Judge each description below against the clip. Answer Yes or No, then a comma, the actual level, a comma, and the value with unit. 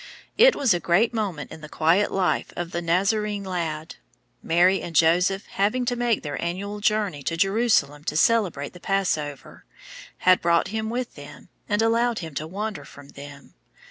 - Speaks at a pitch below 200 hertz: Yes, medium, 185 Hz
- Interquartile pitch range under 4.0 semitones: No, average, 4.7 semitones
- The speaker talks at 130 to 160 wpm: No, average, 175 wpm